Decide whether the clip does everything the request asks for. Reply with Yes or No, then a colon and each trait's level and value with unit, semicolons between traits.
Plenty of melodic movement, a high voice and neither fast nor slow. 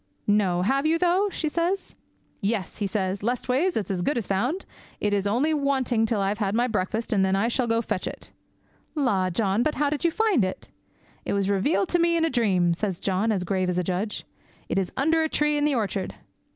No: wide, 7.4 semitones; high, 225 Hz; fast, 235 wpm